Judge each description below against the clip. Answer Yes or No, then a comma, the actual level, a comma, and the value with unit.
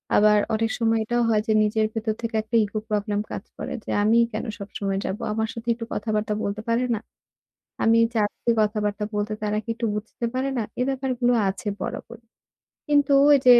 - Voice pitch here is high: Yes, high, 220 Hz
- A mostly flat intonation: Yes, narrow, 1.9 semitones